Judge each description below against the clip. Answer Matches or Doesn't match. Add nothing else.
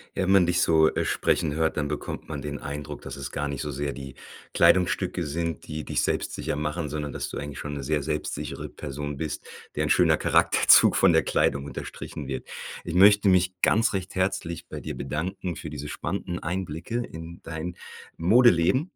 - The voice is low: Matches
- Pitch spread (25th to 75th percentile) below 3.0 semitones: Doesn't match